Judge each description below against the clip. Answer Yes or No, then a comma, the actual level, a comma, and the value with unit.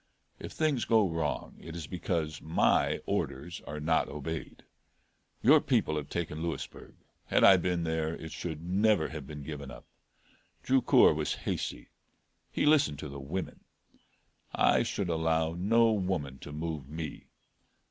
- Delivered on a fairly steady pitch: No, average, 3.3 semitones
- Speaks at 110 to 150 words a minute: Yes, average, 145 wpm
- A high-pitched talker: No, very low, 80 Hz